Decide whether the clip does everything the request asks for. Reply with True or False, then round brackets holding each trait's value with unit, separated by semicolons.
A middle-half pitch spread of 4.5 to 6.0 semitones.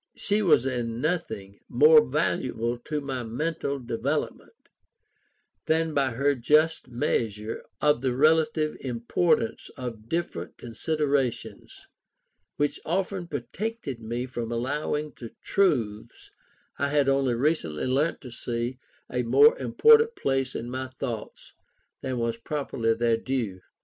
True (4.8 semitones)